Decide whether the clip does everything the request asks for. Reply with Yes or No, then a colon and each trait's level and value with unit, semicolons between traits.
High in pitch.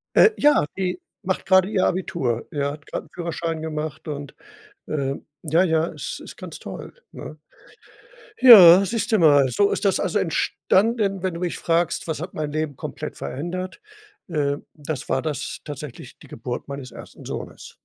No: medium, 165 Hz